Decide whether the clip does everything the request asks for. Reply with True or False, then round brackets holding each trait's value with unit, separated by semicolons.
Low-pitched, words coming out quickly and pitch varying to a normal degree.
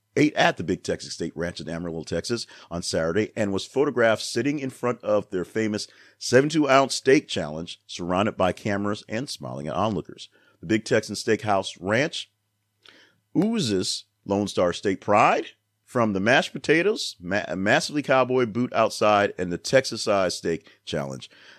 False (105 Hz; 155 wpm; 3.5 semitones)